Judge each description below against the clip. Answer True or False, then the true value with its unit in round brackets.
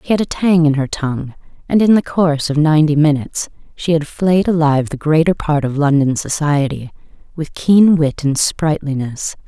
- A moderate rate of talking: True (185 wpm)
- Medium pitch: True (155 Hz)